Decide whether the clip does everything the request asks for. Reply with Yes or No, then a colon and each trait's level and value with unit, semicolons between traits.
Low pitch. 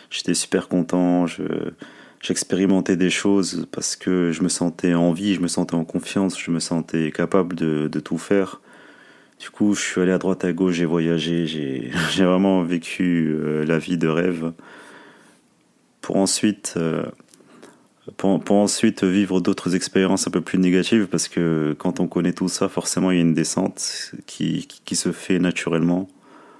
Yes: very low, 90 Hz